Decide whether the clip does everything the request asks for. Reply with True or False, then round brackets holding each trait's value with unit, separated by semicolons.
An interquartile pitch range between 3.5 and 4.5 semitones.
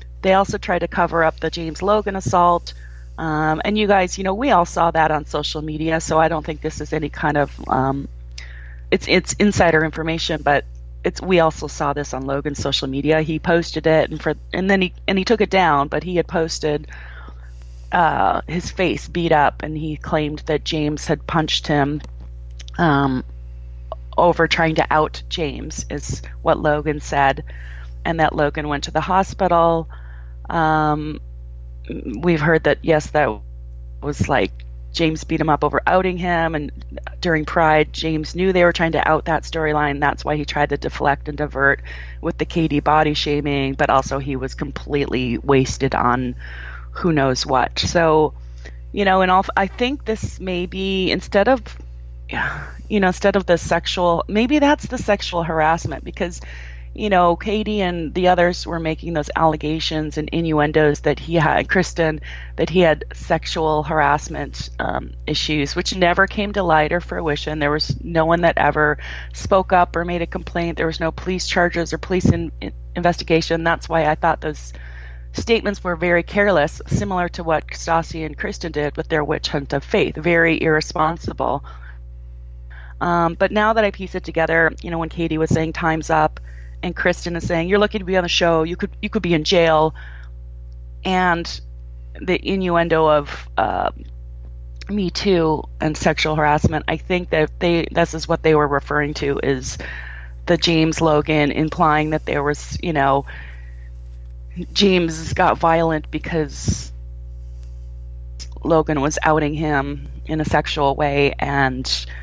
True (4.2 semitones)